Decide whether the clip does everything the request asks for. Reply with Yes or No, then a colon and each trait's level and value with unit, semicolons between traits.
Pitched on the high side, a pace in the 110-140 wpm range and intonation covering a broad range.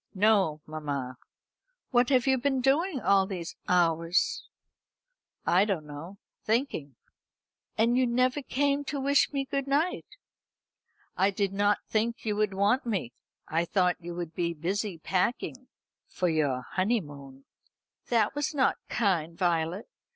Yes: high, 200 Hz; slow, 135 wpm; wide, 7.1 semitones